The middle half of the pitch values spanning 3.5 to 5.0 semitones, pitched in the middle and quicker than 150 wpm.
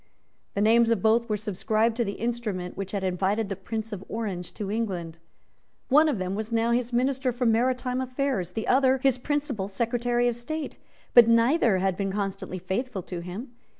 No: average, 4.0 semitones; high, 225 Hz; average, 185 wpm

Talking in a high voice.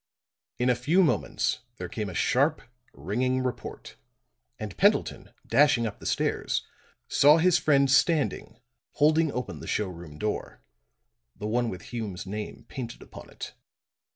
No: low, 125 Hz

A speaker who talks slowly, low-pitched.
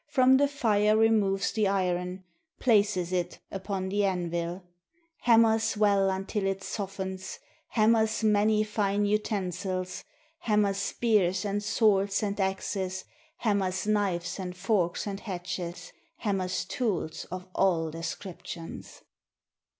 No: slow, 110 wpm; high, 195 Hz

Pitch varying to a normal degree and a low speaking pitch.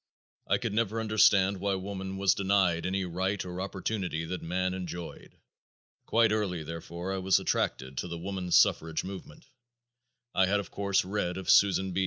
No: narrow, 1.8 semitones; very low, 95 Hz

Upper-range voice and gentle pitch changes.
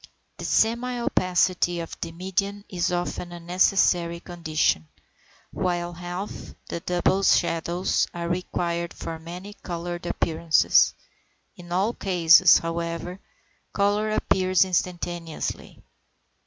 No: medium, 175 Hz; narrow, 1.7 semitones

